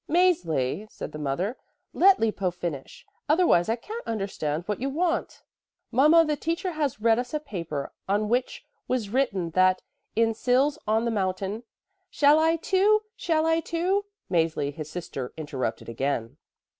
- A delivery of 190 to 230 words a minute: No, average, 155 wpm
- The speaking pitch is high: Yes, high, 225 Hz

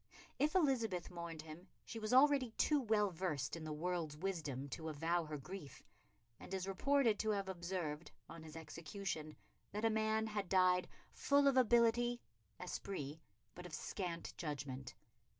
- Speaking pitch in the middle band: Yes, medium, 180 Hz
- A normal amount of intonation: No, wide, 5.7 semitones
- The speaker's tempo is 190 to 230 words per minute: No, average, 155 wpm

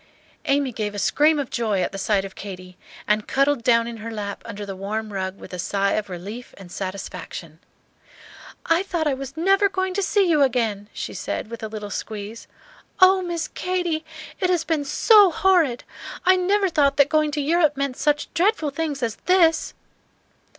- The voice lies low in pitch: No, very high, 275 Hz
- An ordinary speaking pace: Yes, average, 190 wpm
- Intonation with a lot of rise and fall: Yes, wide, 8.1 semitones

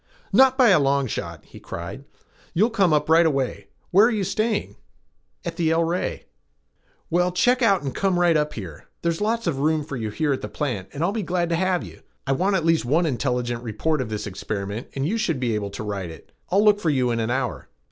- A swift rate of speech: Yes, fast, 235 wpm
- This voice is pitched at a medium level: Yes, medium, 155 Hz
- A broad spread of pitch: Yes, wide, 6.9 semitones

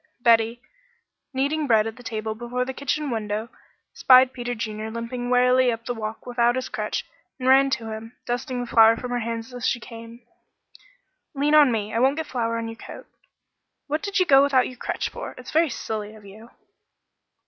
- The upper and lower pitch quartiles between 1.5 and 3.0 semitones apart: Yes, narrow, 2.4 semitones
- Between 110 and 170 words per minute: No, average, 195 wpm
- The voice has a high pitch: Yes, high, 240 Hz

